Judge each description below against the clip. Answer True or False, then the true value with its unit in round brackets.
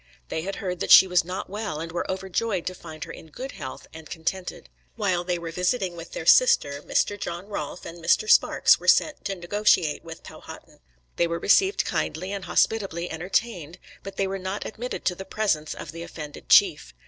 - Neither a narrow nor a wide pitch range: True (3.2 semitones)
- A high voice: False (180 Hz)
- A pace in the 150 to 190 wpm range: False (200 wpm)